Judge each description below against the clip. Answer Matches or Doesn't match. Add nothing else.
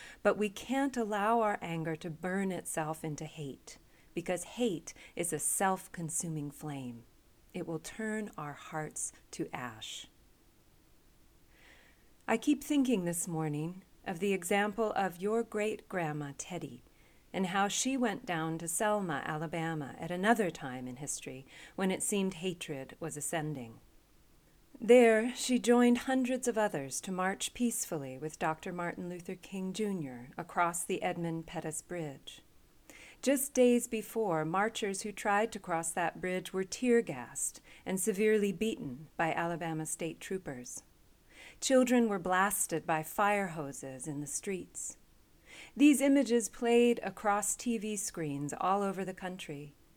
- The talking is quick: Doesn't match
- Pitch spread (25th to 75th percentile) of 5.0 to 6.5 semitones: Matches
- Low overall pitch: Doesn't match